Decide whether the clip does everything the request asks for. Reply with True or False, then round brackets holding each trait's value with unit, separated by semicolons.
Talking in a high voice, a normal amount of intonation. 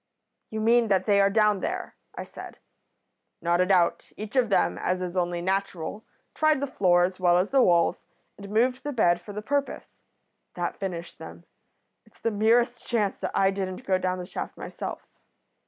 True (200 Hz; 3.9 semitones)